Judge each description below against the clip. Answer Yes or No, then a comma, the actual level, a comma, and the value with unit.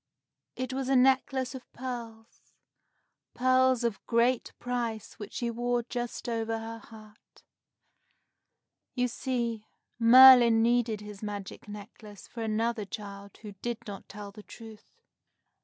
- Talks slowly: Yes, slow, 125 wpm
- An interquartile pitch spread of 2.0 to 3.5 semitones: Yes, narrow, 2.4 semitones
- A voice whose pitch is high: Yes, high, 230 Hz